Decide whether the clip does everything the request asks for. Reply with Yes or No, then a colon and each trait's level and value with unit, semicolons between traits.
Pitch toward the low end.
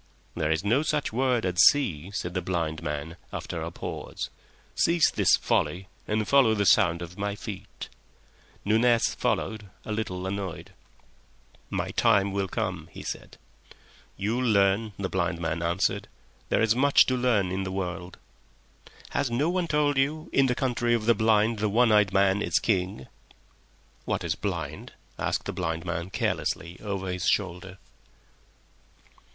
Yes: low, 100 Hz